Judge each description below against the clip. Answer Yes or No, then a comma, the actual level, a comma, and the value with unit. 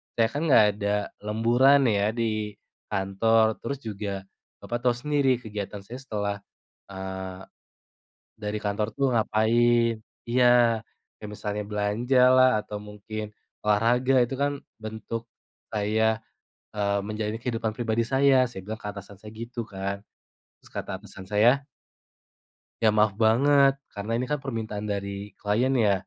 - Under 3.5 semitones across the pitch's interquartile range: Yes, average, 2.8 semitones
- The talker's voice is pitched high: No, low, 110 Hz